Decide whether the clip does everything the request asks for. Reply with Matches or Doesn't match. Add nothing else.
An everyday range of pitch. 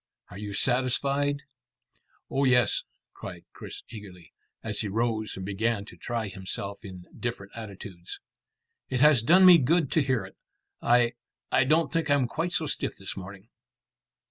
Doesn't match